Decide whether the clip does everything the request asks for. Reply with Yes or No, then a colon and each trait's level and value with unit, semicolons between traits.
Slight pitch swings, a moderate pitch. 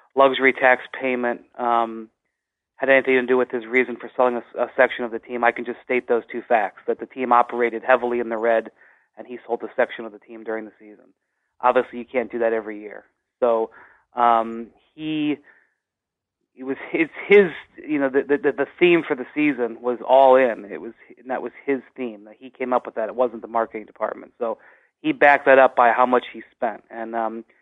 No: narrow, 2.3 semitones; low, 125 Hz